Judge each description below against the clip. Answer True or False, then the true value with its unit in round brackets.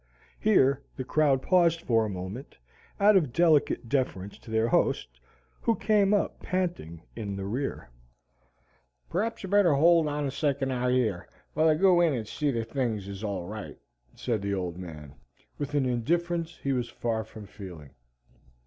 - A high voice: False (130 Hz)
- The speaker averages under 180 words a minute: True (170 wpm)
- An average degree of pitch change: False (8.0 semitones)